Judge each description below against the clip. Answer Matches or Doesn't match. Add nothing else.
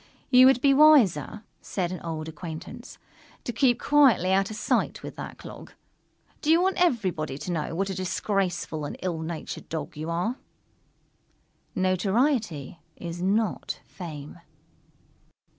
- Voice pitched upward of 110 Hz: Matches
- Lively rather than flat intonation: Matches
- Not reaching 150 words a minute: Matches